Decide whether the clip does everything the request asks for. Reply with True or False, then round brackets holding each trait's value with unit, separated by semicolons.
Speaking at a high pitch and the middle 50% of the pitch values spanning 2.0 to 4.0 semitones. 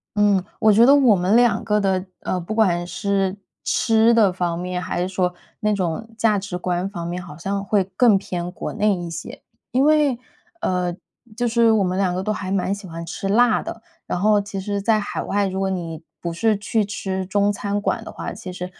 True (195 Hz; 2.8 semitones)